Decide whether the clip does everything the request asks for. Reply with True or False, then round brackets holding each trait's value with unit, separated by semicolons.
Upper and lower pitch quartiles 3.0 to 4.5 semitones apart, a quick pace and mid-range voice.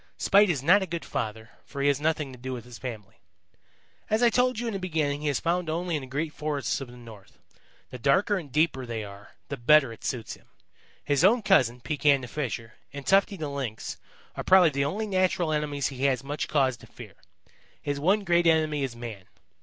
False (5.3 semitones; 220 wpm; 145 Hz)